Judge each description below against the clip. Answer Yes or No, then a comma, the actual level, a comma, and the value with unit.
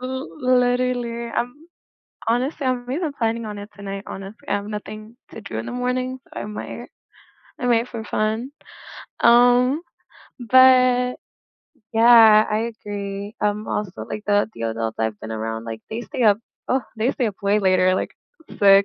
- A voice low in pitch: No, high, 225 Hz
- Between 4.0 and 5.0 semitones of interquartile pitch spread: No, average, 3.5 semitones